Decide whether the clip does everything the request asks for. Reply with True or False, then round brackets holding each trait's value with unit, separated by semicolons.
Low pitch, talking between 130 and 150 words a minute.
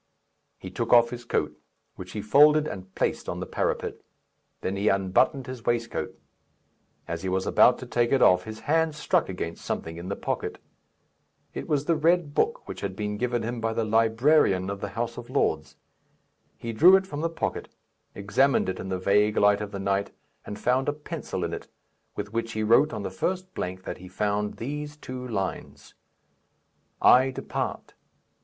False (115 Hz; 190 wpm)